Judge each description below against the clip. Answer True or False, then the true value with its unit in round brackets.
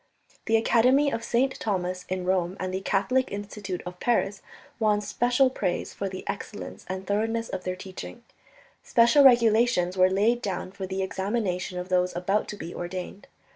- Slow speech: False (170 wpm)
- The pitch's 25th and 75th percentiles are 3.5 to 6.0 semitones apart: True (3.8 semitones)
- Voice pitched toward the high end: True (195 Hz)